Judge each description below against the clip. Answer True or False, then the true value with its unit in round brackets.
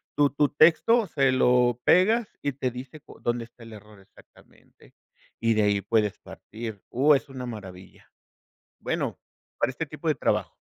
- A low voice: True (125 Hz)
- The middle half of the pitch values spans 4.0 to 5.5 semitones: True (4.7 semitones)